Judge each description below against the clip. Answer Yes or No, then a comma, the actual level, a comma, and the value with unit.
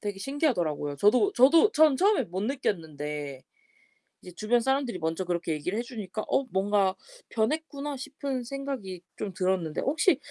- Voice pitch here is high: Yes, high, 215 Hz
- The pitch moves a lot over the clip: Yes, wide, 7.5 semitones